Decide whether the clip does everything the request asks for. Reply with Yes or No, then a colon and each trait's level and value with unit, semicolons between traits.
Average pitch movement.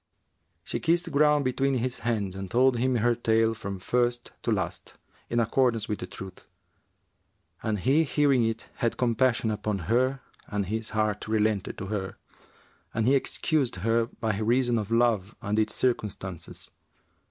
Yes: average, 3.1 semitones